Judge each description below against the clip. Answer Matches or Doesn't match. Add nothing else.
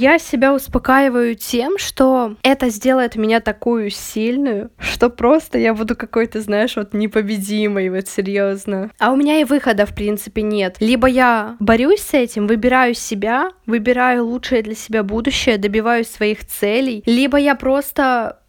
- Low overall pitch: Doesn't match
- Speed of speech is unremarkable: Matches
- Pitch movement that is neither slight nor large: Matches